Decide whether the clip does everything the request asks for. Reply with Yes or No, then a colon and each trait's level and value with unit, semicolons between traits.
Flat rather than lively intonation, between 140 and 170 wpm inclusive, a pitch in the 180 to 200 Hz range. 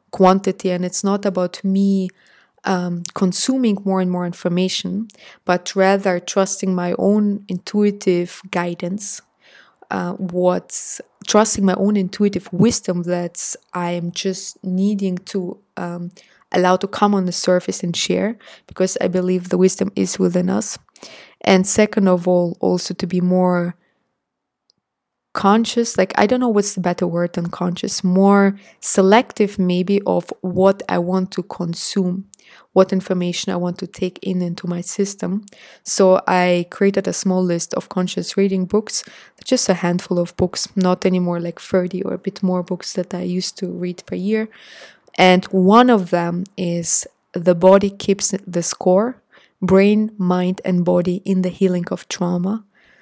Yes: narrow, 1.7 semitones; average, 155 wpm; medium, 185 Hz